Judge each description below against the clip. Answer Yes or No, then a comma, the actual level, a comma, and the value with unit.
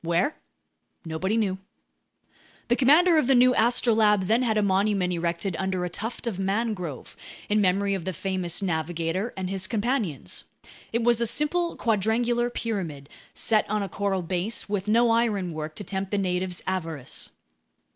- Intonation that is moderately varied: Yes, average, 4.1 semitones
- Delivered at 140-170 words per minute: Yes, average, 155 wpm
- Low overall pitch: No, high, 200 Hz